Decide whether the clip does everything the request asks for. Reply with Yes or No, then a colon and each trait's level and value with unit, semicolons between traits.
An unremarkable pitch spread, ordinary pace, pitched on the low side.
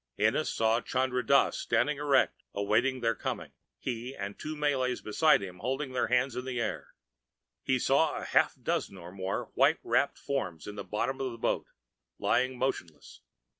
Yes: average, 4.1 semitones; average, 175 wpm; low, 125 Hz